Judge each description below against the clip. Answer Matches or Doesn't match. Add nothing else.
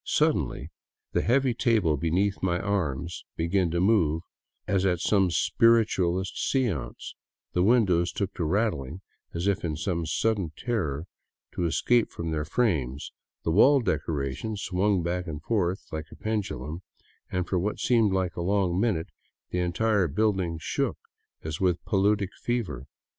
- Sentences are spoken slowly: Doesn't match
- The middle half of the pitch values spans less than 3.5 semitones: Doesn't match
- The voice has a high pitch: Doesn't match